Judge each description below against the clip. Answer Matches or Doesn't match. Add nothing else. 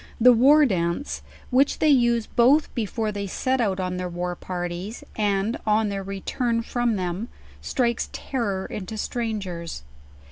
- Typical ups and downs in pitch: Matches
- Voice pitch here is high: Matches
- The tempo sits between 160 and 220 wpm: Doesn't match